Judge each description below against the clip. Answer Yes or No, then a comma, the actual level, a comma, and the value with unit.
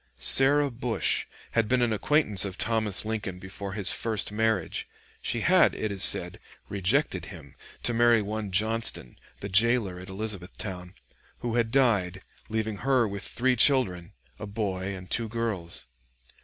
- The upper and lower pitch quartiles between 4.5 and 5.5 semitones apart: No, average, 3.4 semitones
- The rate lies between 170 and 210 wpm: No, average, 150 wpm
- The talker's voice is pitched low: Yes, low, 110 Hz